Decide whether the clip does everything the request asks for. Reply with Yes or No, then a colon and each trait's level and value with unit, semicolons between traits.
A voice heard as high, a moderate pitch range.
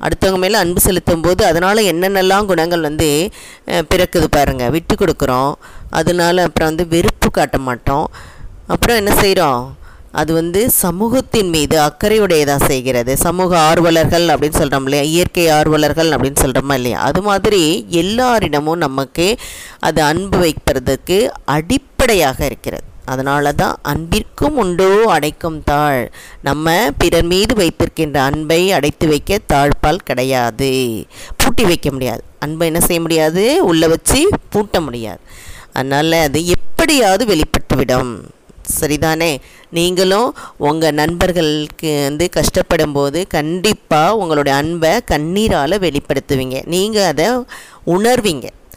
No: medium, 160 Hz; average, 3.9 semitones